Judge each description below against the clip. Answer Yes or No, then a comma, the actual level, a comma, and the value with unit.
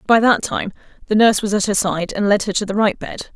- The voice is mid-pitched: No, high, 205 Hz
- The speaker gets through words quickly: Yes, fast, 285 wpm